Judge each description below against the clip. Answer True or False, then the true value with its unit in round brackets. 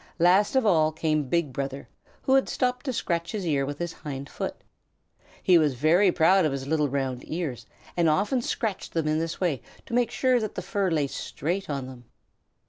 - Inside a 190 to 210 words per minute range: True (205 wpm)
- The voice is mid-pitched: True (165 Hz)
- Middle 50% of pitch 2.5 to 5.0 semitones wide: False (5.4 semitones)